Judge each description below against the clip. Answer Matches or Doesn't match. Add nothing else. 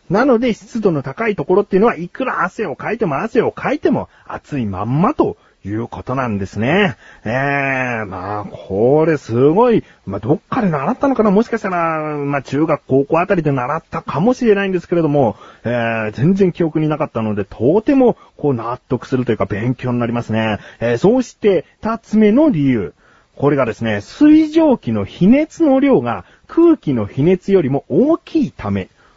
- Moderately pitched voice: Matches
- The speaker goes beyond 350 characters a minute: Matches